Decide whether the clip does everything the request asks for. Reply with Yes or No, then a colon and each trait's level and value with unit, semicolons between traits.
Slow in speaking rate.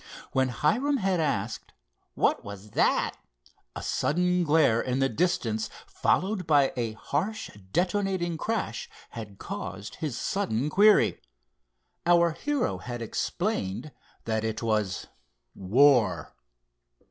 Yes: slow, 110 wpm